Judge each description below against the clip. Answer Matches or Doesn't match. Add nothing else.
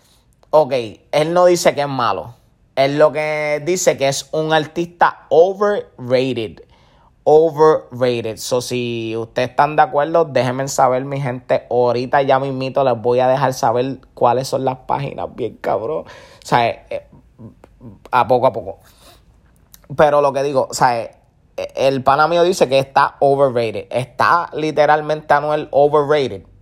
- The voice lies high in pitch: Doesn't match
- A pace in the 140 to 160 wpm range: Matches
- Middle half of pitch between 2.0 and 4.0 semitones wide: Matches